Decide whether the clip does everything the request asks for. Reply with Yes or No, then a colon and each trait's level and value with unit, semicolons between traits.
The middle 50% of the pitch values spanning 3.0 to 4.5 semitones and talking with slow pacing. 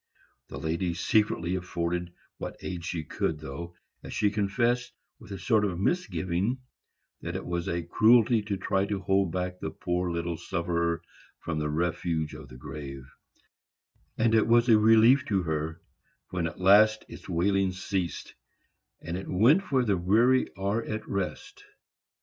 No: average, 4.1 semitones; average, 160 wpm